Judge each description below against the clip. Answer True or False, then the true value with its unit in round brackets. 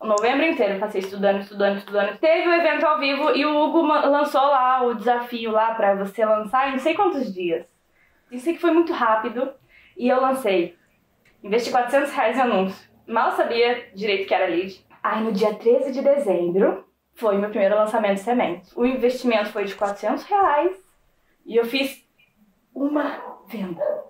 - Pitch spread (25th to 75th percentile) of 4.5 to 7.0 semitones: True (5.5 semitones)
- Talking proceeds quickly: False (175 wpm)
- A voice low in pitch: False (240 Hz)